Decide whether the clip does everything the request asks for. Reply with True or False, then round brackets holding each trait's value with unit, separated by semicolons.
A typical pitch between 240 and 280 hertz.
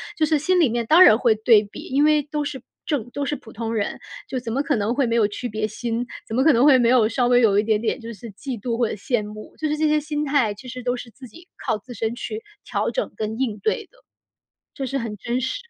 True (245 Hz)